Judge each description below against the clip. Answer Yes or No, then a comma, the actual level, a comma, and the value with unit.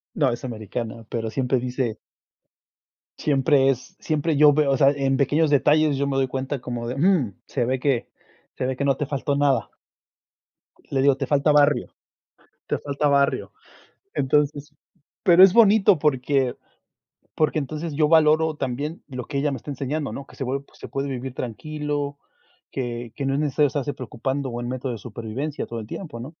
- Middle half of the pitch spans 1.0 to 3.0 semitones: Yes, narrow, 2.6 semitones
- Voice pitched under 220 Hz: Yes, medium, 140 Hz